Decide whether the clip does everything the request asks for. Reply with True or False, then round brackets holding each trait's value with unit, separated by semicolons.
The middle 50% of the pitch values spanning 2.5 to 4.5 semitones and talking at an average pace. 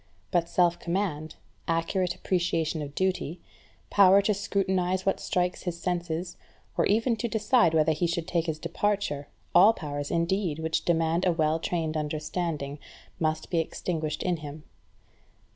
True (2.8 semitones; 145 wpm)